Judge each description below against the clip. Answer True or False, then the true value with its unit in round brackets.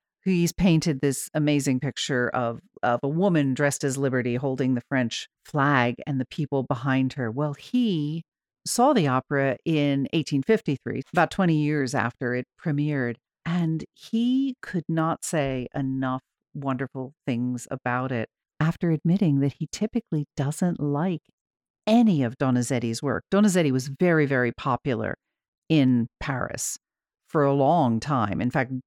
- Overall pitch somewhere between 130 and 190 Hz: True (140 Hz)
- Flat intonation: False (3.9 semitones)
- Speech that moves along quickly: False (140 wpm)